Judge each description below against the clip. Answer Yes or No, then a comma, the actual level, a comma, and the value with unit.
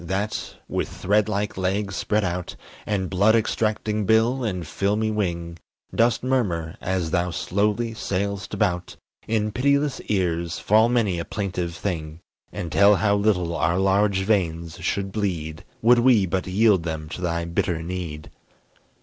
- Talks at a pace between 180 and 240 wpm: No, average, 150 wpm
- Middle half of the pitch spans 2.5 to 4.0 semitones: Yes, average, 3.7 semitones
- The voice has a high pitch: No, very low, 95 Hz